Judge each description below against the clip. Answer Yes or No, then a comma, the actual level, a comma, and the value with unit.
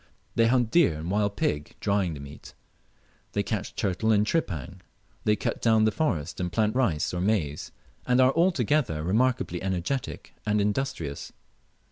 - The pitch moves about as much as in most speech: No, wide, 6.2 semitones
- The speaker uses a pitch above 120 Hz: No, low, 105 Hz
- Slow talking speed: No, average, 155 wpm